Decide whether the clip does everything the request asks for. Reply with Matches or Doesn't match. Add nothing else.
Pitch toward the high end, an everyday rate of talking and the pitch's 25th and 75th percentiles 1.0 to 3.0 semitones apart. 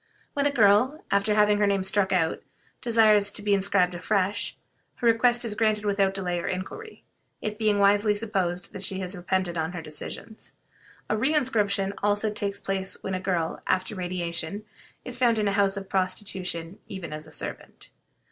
Matches